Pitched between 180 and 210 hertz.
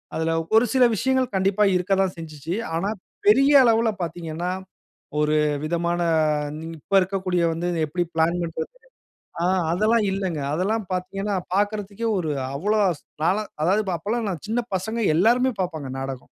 Yes: medium, 185 Hz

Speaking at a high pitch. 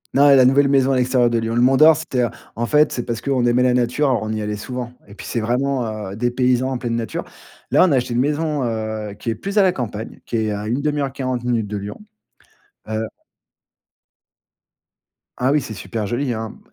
No: low, 120 Hz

